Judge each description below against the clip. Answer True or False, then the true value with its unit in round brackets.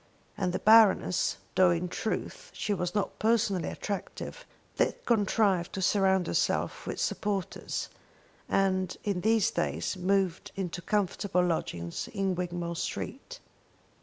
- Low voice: False (190 Hz)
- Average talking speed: False (125 wpm)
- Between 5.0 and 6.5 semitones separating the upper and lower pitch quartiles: False (2.5 semitones)